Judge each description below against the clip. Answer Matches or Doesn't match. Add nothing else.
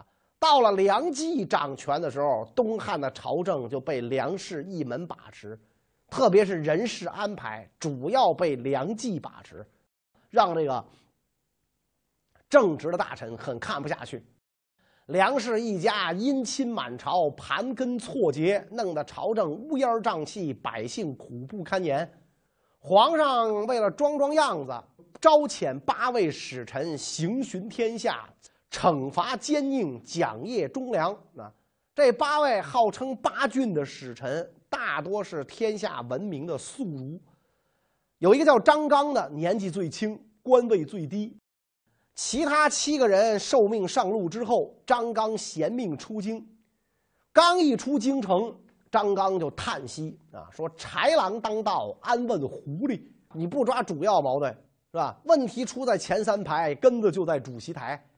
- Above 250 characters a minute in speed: Doesn't match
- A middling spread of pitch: Doesn't match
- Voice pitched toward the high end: Matches